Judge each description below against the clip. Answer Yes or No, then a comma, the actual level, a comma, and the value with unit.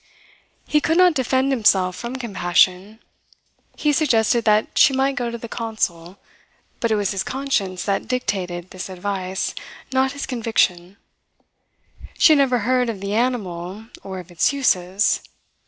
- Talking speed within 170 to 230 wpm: No, average, 150 wpm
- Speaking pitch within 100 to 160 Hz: No, high, 220 Hz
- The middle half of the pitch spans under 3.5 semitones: No, wide, 5.5 semitones